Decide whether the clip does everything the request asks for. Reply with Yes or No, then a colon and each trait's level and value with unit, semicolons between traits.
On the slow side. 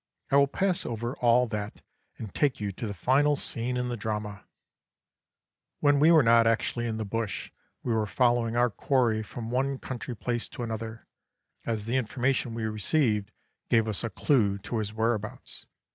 No: average, 175 wpm